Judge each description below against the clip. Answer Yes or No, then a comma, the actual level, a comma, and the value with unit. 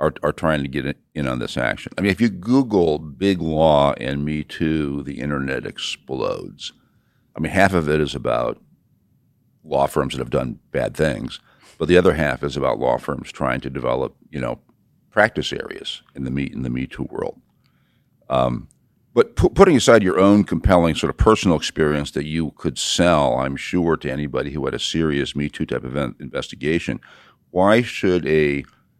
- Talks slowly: No, average, 190 wpm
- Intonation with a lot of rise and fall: No, average, 3.4 semitones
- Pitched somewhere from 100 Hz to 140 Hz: No, very low, 75 Hz